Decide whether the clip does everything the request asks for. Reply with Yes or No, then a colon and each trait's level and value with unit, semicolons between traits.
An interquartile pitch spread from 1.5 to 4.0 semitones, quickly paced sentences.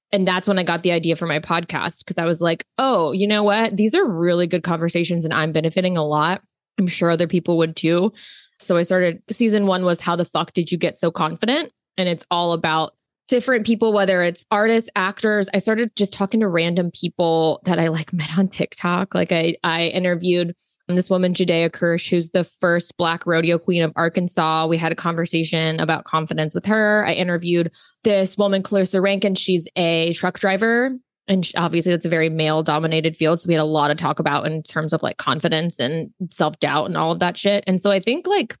Yes: average, 2.8 semitones; fast, 215 wpm